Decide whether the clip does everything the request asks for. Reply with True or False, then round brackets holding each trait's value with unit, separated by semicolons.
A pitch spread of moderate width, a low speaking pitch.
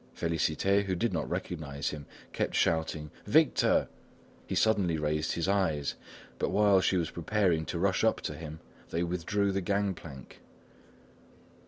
True (4.0 semitones; 85 Hz)